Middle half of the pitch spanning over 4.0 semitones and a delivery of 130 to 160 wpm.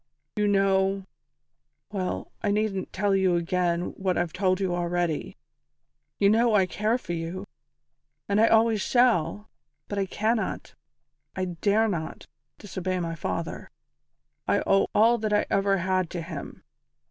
No: average, 2.9 semitones; average, 145 wpm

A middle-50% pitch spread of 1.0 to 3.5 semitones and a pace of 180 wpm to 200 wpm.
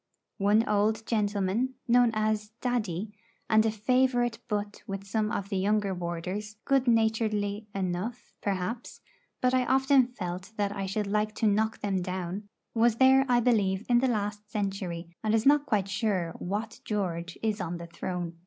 No: average, 2.9 semitones; average, 165 wpm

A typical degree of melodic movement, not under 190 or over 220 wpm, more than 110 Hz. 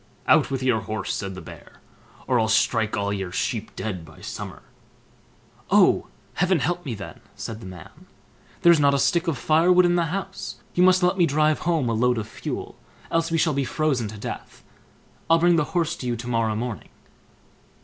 No: wide, 7.2 semitones; average, 200 wpm; low, 135 Hz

